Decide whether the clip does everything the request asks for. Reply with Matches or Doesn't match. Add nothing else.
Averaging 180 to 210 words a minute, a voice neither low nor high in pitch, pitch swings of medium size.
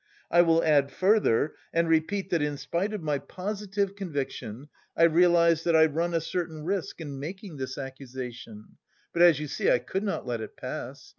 Matches